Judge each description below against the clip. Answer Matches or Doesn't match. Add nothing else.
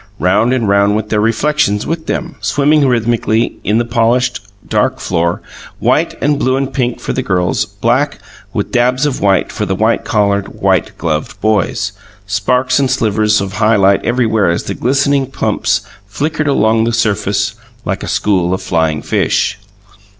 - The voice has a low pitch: Matches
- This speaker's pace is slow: Doesn't match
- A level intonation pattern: Doesn't match